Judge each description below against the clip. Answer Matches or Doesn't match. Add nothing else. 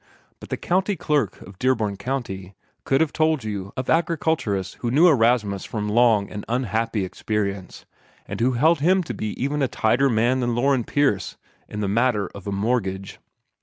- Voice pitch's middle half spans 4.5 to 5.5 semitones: Matches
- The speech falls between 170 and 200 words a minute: Matches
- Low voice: Matches